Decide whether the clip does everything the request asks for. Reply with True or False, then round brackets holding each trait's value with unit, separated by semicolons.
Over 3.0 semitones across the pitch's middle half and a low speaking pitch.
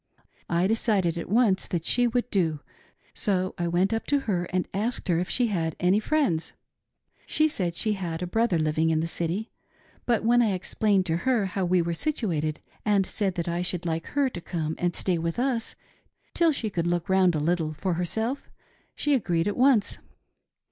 False (4.7 semitones; 185 Hz)